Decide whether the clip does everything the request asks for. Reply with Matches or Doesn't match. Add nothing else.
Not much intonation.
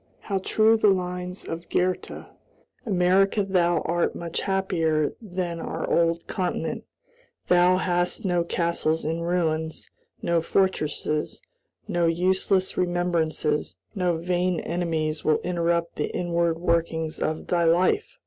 Matches